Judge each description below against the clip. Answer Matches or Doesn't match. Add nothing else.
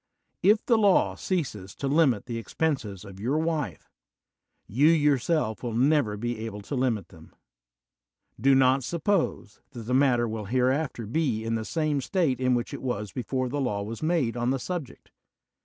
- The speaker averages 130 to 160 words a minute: Doesn't match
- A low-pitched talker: Matches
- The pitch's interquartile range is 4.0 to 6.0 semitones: Matches